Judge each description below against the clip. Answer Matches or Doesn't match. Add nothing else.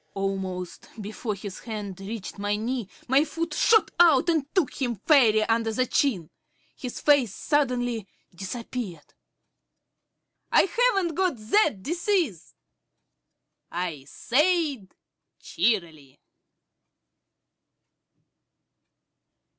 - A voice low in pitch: Doesn't match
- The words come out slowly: Matches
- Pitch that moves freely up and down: Matches